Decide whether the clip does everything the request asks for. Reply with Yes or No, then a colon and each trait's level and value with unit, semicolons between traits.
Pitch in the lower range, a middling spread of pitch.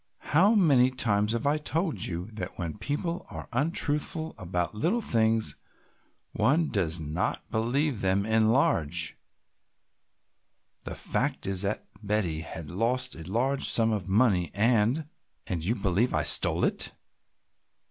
No: low, 110 Hz; wide, 6.6 semitones